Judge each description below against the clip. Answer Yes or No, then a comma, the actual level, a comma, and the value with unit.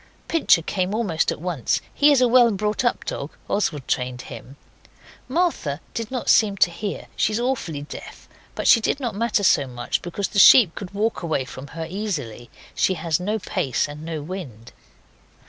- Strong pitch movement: Yes, wide, 7.1 semitones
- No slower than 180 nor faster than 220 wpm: Yes, average, 185 wpm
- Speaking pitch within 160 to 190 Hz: Yes, medium, 185 Hz